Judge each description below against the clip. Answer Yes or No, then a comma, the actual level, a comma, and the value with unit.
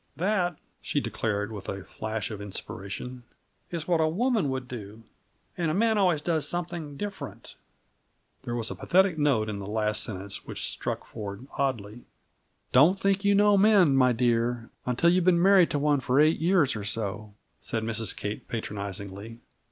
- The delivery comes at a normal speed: Yes, average, 170 wpm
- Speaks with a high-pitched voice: No, low, 130 Hz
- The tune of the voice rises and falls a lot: Yes, wide, 8.2 semitones